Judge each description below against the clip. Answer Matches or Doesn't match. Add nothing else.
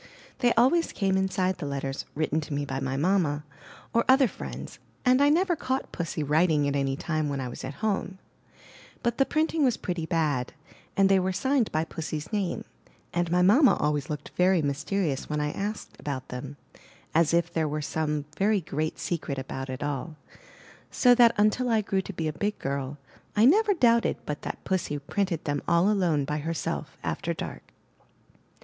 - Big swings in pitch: Matches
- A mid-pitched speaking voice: Matches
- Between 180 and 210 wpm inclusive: Matches